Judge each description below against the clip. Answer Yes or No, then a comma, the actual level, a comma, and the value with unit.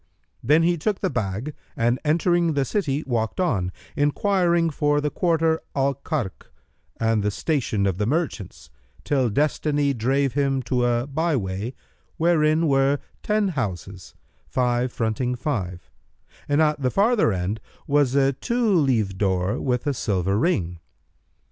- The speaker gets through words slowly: No, average, 145 wpm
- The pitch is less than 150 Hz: Yes, low, 135 Hz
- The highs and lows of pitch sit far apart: Yes, wide, 6.0 semitones